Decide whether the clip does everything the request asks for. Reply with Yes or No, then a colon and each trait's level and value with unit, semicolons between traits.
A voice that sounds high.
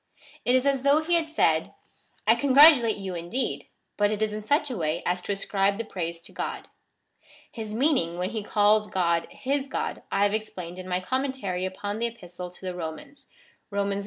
Yes: high, 205 Hz